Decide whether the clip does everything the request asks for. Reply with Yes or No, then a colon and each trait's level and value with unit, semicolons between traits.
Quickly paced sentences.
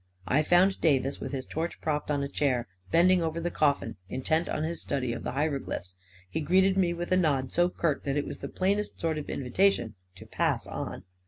Yes: fast, 215 wpm